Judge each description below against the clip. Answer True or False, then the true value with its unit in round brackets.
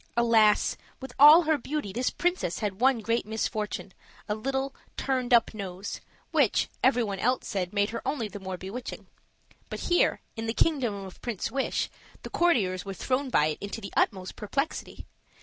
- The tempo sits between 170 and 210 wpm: True (175 wpm)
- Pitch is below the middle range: False (225 Hz)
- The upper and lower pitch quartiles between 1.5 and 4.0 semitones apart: False (4.8 semitones)